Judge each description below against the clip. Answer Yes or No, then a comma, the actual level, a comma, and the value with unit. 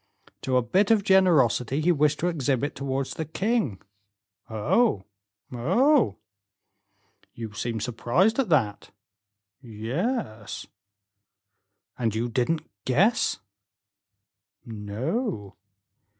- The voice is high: No, low, 135 Hz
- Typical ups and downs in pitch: No, wide, 8.6 semitones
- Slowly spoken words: Yes, slow, 95 wpm